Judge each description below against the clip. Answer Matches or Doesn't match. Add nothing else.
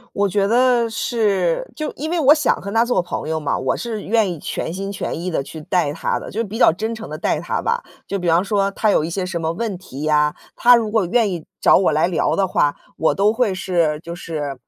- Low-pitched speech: Doesn't match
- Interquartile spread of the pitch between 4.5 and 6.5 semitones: Matches